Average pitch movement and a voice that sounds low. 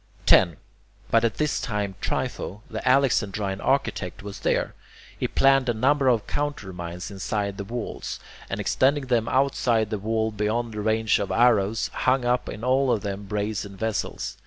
Yes: average, 3.8 semitones; low, 110 Hz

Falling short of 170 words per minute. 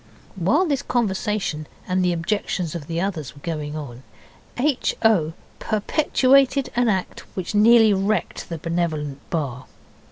Yes: slow, 135 wpm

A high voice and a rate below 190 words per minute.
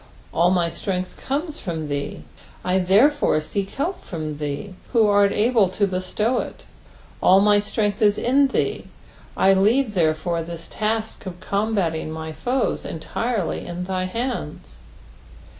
Yes: high, 195 Hz; average, 140 wpm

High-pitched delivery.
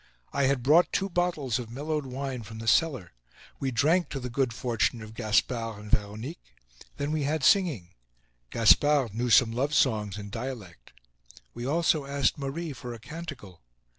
No: low, 130 Hz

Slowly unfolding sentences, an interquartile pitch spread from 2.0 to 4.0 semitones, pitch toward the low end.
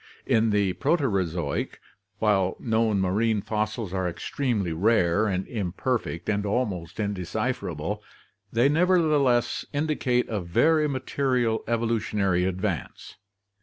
No: slow, 100 wpm; average, 4.7 semitones; low, 110 Hz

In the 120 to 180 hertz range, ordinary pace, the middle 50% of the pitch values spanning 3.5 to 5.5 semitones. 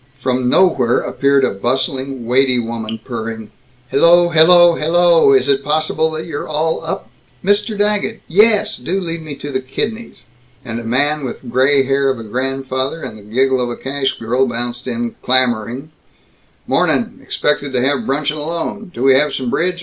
Yes: low, 135 Hz; average, 175 wpm; average, 4.3 semitones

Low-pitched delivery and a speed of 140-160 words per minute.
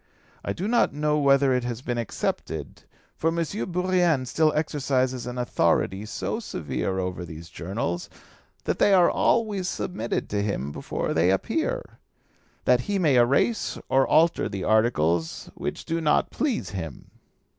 Yes: low, 130 Hz; average, 150 wpm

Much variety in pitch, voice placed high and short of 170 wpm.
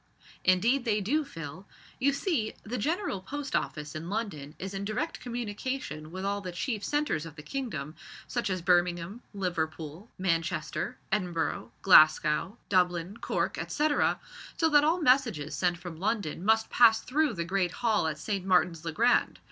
Yes: wide, 6.1 semitones; high, 195 Hz; average, 160 wpm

